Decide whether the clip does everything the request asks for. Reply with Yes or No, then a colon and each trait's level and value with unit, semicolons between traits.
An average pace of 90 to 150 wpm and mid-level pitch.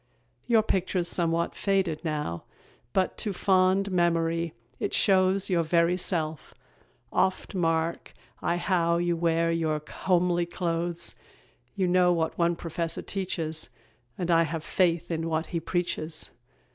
Yes: slow, 135 wpm; medium, 170 Hz